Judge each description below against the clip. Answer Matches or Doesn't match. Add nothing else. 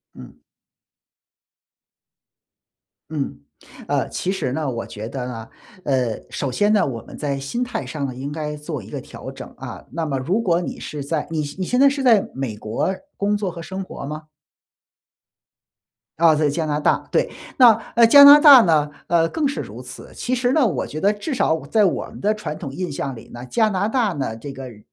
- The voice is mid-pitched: Matches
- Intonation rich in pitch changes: Matches